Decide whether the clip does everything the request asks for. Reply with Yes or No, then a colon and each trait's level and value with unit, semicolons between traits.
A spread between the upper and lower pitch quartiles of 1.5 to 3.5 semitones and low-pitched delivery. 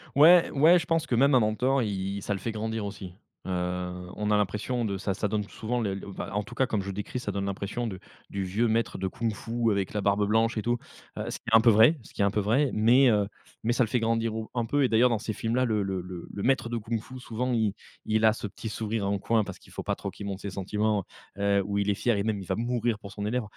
Yes: average, 2.8 semitones; low, 110 Hz